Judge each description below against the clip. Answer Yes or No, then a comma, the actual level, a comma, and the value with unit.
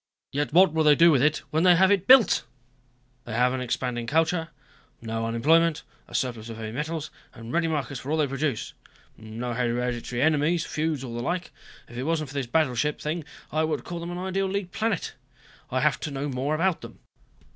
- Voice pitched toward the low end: No, medium, 150 Hz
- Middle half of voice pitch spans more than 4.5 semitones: Yes, average, 5.0 semitones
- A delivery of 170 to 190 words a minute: No, fast, 205 wpm